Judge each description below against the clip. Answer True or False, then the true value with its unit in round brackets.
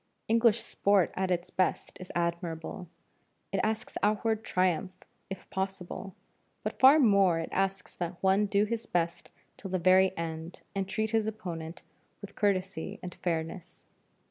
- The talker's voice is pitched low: False (190 Hz)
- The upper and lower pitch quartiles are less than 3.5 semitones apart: True (3.1 semitones)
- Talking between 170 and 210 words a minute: False (145 wpm)